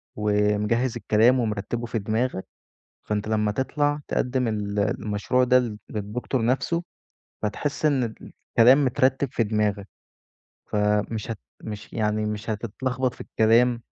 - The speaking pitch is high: No, low, 110 Hz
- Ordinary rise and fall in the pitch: Yes, average, 3.2 semitones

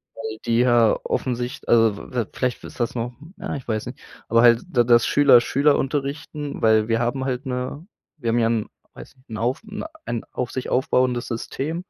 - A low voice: Yes, low, 125 Hz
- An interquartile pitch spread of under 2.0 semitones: No, narrow, 2.6 semitones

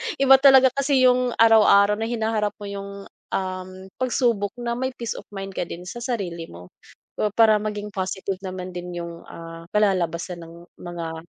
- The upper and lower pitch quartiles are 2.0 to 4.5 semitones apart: No, average, 4.9 semitones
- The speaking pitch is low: No, high, 200 Hz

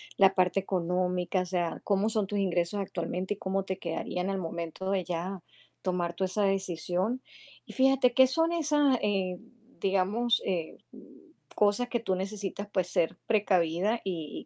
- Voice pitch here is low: No, high, 190 Hz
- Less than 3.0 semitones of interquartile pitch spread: Yes, narrow, 2.5 semitones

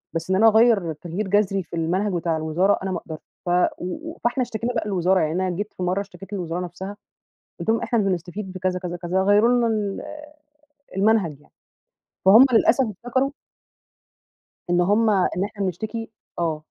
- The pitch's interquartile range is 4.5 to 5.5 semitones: No, average, 3.6 semitones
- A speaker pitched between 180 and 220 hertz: Yes, high, 190 Hz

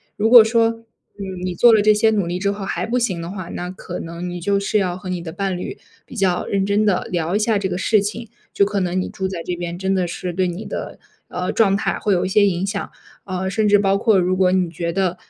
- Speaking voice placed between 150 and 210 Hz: Yes, high, 190 Hz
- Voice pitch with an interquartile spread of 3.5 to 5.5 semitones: No, narrow, 2.5 semitones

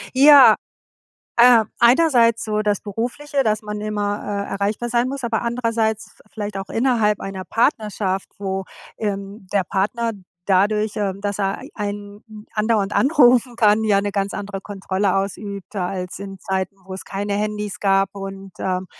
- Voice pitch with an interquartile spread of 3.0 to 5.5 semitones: No, narrow, 2.6 semitones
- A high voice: Yes, high, 205 Hz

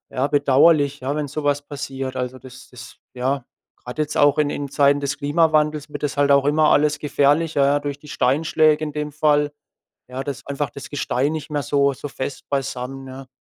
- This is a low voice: No, medium, 145 Hz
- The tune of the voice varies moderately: No, narrow, 1.8 semitones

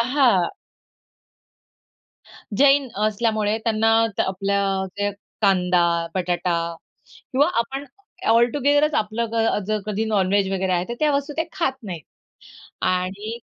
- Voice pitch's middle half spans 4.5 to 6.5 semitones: Yes, average, 5.0 semitones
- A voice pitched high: Yes, high, 215 Hz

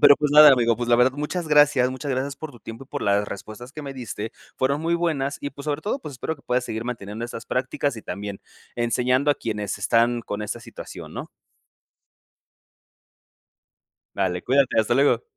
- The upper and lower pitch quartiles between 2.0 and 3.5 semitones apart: No, average, 3.9 semitones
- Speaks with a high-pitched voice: No, low, 125 Hz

